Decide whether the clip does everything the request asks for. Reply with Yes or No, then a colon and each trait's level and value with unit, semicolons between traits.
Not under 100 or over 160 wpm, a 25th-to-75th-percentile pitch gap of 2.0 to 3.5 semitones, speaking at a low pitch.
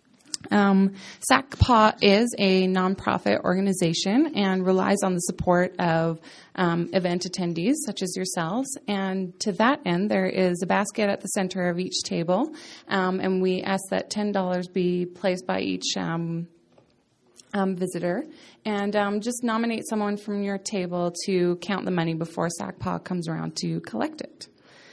No: average, 155 wpm; narrow, 2.4 semitones; high, 190 Hz